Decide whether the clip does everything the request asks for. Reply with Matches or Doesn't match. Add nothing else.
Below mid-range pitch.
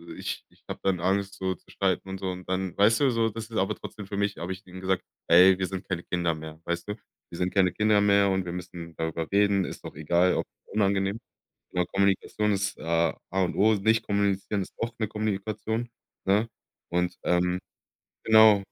Matches